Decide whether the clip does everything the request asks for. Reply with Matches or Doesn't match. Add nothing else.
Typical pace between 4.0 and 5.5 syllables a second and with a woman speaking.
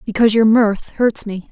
Matches